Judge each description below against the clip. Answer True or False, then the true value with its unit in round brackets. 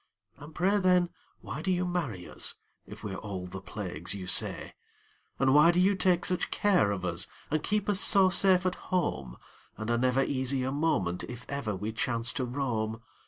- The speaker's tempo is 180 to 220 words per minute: True (195 wpm)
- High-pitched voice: False (130 Hz)